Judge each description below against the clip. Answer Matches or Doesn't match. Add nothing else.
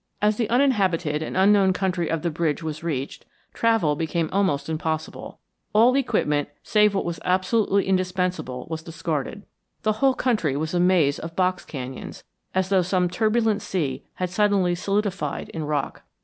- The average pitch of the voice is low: Doesn't match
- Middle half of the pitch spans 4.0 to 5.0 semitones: Matches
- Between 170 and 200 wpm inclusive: Doesn't match